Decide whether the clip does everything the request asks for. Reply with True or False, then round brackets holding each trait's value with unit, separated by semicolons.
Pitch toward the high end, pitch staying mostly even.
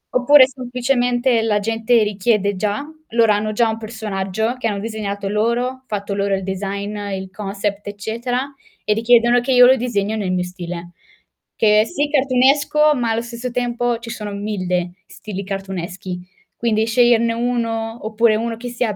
False (225 Hz; 3.2 semitones)